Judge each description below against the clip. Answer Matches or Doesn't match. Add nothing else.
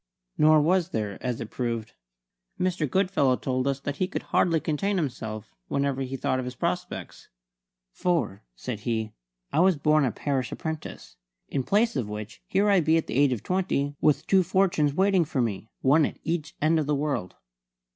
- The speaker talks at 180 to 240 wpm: Matches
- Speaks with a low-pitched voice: Doesn't match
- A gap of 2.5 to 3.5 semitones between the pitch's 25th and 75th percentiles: Doesn't match